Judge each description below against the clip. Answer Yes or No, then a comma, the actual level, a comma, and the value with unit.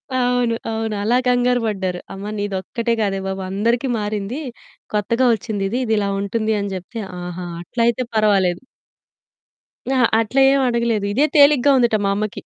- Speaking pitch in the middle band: No, high, 220 Hz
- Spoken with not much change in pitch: No, average, 3.4 semitones